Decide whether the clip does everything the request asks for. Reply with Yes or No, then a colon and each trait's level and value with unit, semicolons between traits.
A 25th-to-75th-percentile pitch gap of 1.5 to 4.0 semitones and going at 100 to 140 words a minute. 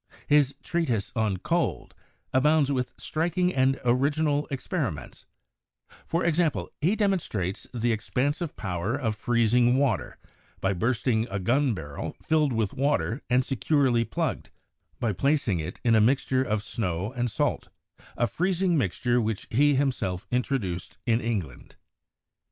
No: average, 4.8 semitones; slow, 135 wpm